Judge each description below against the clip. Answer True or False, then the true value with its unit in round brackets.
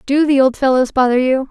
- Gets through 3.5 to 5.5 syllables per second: False (5.8 syllables/s)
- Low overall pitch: False (265 Hz)